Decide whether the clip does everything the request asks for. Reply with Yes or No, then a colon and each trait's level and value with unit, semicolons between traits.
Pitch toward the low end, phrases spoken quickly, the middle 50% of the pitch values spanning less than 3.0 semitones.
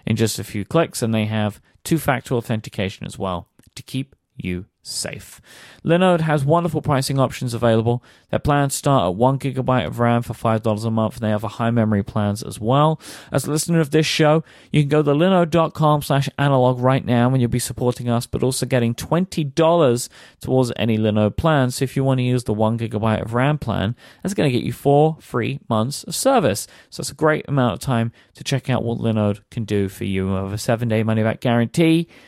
No: low, 125 Hz; fast, 220 wpm; average, 4.7 semitones